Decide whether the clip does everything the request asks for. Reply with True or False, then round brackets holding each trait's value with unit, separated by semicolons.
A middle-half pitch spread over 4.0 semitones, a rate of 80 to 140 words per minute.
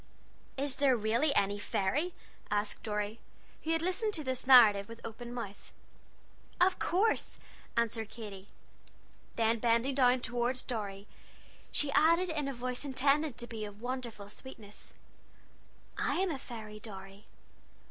True (4.6 semitones; 135 wpm)